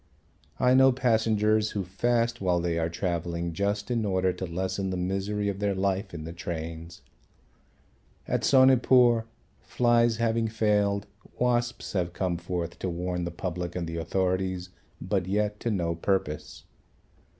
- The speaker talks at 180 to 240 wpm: No, average, 150 wpm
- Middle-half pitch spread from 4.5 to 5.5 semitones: No, average, 4.0 semitones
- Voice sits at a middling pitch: No, very low, 95 Hz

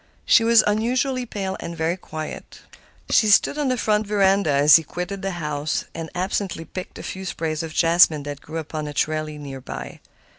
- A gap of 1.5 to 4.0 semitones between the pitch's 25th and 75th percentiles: No, average, 4.7 semitones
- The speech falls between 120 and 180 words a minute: No, average, 190 wpm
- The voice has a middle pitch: Yes, medium, 170 Hz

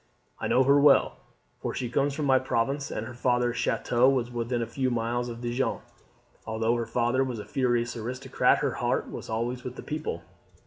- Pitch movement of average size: No, narrow, 1.9 semitones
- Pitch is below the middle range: Yes, low, 120 Hz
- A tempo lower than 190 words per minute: No, average, 195 wpm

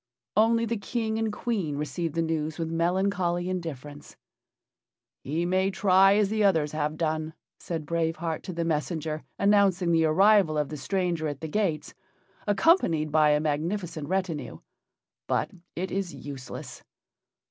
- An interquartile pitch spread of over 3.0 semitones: Yes, average, 3.9 semitones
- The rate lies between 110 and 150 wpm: Yes, average, 145 wpm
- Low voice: No, medium, 170 Hz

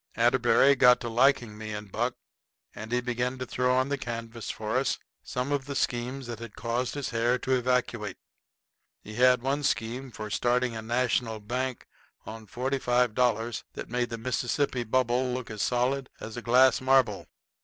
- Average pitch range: No, narrow, 1.9 semitones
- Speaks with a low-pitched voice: Yes, low, 125 Hz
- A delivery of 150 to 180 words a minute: Yes, average, 175 wpm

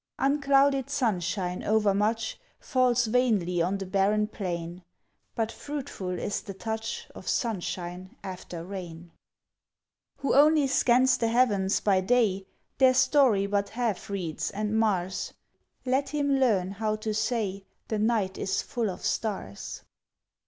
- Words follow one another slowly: Yes, slow, 130 wpm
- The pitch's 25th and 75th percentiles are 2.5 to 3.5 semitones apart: No, average, 4.7 semitones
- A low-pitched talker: No, high, 215 Hz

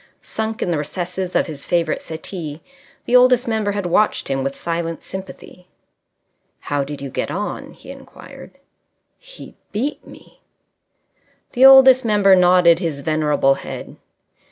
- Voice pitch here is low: No, medium, 180 Hz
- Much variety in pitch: Yes, wide, 5.7 semitones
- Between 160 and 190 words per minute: No, average, 140 wpm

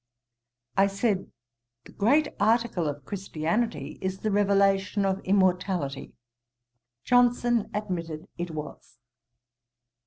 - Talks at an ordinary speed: No, slow, 100 wpm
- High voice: Yes, high, 195 Hz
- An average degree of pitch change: Yes, average, 4.2 semitones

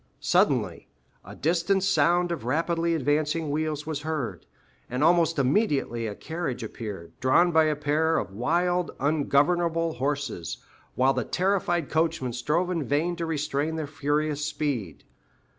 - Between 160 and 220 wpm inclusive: No, average, 140 wpm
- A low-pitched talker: No, medium, 155 Hz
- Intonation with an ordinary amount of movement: Yes, average, 3.3 semitones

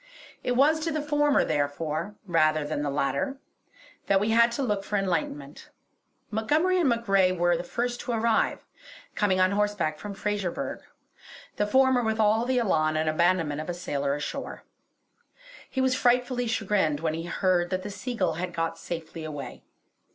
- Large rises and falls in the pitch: Yes, wide, 6.4 semitones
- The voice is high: Yes, high, 195 Hz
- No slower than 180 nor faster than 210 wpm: No, average, 165 wpm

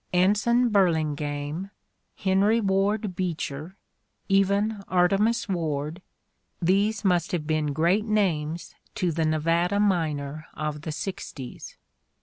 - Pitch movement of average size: Yes, average, 4.3 semitones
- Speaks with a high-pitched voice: No, medium, 180 Hz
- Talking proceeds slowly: Yes, slow, 110 wpm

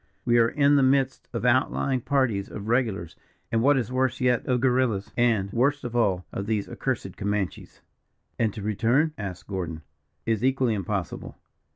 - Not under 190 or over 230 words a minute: No, average, 175 wpm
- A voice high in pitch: No, low, 115 Hz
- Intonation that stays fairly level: No, average, 4.2 semitones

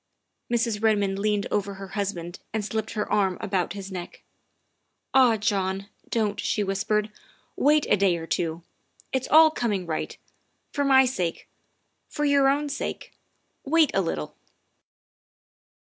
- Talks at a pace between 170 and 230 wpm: No, average, 145 wpm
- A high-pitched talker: Yes, high, 205 Hz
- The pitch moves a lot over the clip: No, average, 4.3 semitones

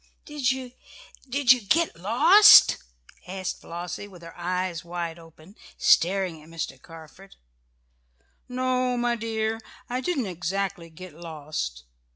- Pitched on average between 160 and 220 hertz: Yes, medium, 185 Hz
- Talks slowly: Yes, slow, 125 wpm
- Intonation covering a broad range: Yes, wide, 6.6 semitones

